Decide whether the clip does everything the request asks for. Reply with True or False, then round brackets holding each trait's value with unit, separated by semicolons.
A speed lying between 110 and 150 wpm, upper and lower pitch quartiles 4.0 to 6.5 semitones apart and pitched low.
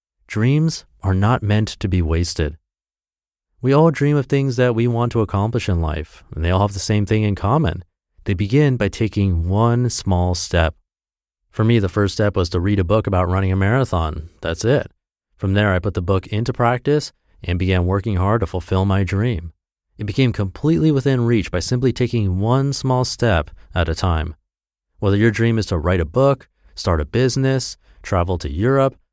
False (195 wpm; 5.1 semitones; 100 Hz)